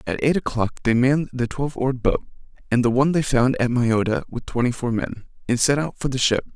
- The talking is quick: Yes, fast, 240 wpm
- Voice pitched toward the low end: Yes, low, 125 Hz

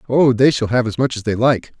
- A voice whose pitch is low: Yes, low, 120 Hz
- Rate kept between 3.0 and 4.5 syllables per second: No, 5.7 syllables/s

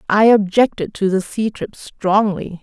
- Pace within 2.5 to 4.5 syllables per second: Yes, 4.1 syllables/s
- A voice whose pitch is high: Yes, high, 205 Hz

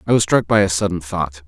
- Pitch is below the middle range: Yes, very low, 90 Hz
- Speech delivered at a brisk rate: Yes, fast, 285 wpm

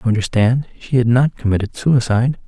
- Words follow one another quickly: No, average, 170 wpm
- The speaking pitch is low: Yes, low, 120 Hz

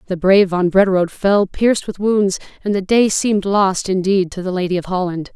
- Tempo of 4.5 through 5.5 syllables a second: No, 5.7 syllables/s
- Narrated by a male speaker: No, female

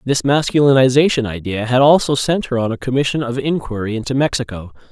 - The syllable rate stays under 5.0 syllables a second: No, 6.1 syllables/s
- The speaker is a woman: No, male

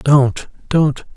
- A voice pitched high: No, medium, 140 Hz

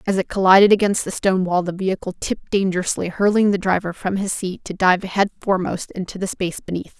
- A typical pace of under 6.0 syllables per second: No, 6.2 syllables/s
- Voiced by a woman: Yes, female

